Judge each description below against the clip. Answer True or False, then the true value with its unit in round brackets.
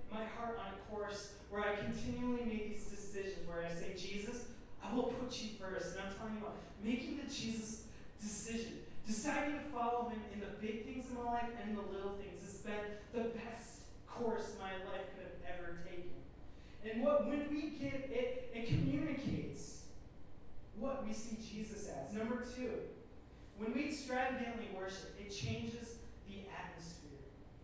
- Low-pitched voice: False (220 Hz)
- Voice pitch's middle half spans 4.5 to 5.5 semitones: False (3.7 semitones)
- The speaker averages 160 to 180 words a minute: True (170 wpm)